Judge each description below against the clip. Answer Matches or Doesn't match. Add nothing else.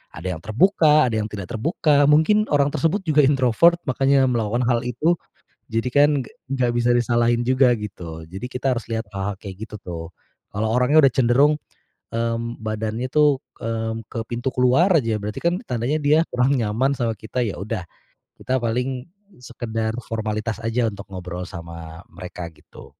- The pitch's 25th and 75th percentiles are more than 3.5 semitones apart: Matches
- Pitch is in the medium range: Doesn't match